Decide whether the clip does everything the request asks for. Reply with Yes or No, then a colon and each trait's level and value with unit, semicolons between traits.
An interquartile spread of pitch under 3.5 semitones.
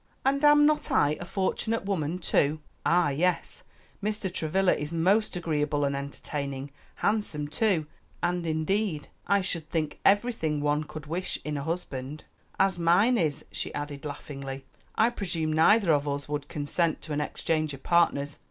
No: average, 4.5 semitones